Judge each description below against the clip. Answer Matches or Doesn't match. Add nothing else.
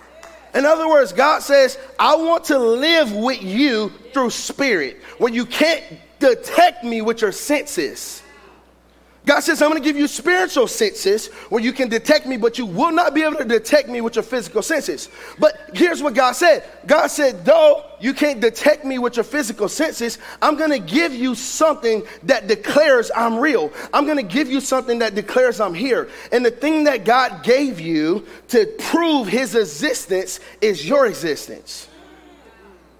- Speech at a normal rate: Matches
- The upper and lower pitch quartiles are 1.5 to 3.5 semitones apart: Doesn't match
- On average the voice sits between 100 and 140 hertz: Doesn't match